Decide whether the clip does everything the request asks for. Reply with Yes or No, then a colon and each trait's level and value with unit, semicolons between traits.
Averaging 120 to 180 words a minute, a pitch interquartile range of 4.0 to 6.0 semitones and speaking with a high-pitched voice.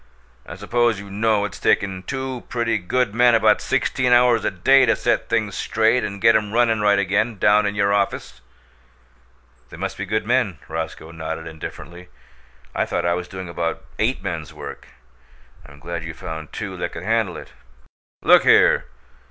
No: average, 175 wpm; average, 4.7 semitones; low, 100 Hz